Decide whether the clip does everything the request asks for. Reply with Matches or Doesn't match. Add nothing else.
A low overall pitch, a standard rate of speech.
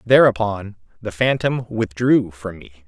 Doesn't match